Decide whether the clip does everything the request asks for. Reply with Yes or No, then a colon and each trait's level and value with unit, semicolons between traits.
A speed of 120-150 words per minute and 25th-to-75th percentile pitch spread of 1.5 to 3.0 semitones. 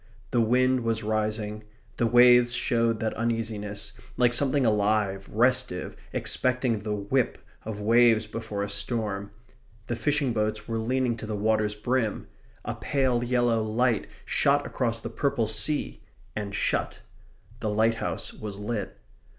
Yes: average, 140 wpm; narrow, 2.4 semitones